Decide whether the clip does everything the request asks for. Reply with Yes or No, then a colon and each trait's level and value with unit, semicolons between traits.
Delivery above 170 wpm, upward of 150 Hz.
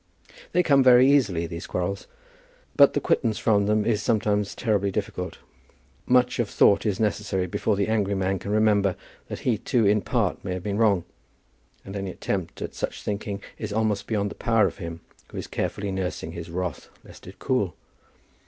No: average, 185 wpm; low, 100 Hz